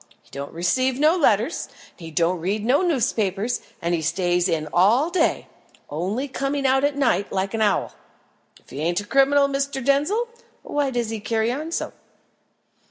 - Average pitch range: No, wide, 7.1 semitones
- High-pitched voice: Yes, high, 235 Hz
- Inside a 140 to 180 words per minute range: Yes, average, 165 wpm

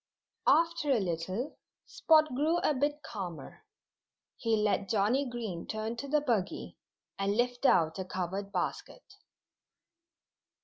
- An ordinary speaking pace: No, slow, 125 wpm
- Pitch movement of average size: No, wide, 6.7 semitones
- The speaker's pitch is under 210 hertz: No, high, 225 Hz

